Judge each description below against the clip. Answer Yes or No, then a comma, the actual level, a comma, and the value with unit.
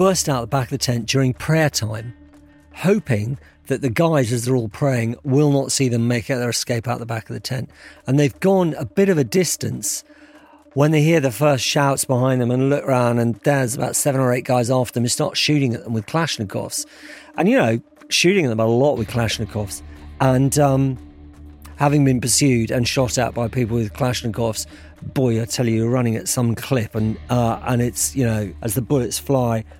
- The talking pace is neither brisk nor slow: No, fast, 215 wpm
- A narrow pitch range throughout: No, average, 3.7 semitones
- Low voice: Yes, low, 125 Hz